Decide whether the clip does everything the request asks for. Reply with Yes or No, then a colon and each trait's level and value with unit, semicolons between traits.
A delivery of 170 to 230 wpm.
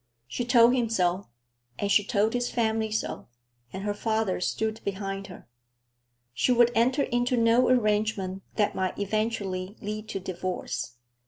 No: average, 150 wpm